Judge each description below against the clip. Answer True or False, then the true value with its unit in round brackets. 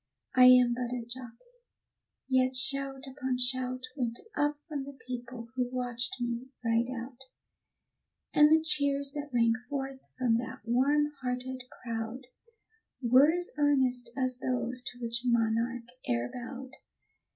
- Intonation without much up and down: True (2.0 semitones)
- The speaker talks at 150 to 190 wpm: False (140 wpm)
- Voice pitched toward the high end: True (255 Hz)